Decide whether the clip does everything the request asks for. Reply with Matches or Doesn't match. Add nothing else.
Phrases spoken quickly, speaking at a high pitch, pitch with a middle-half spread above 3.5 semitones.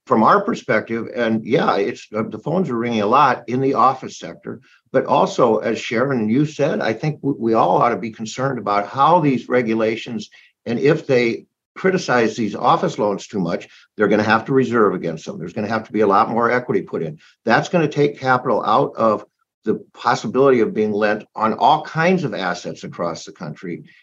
Doesn't match